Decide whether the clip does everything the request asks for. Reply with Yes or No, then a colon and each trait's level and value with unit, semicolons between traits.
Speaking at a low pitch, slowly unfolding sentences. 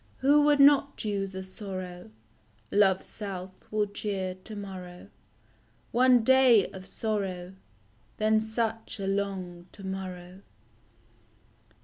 No: high, 200 Hz; slow, 110 wpm